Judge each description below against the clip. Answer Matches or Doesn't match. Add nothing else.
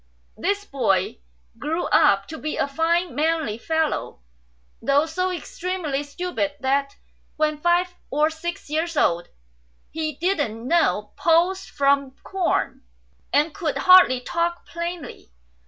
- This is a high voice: Matches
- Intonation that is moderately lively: Matches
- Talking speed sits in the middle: Doesn't match